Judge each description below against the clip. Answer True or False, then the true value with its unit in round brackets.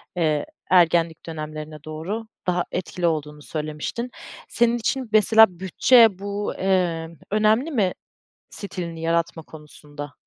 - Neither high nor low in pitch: True (175 Hz)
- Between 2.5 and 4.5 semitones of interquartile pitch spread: False (5.0 semitones)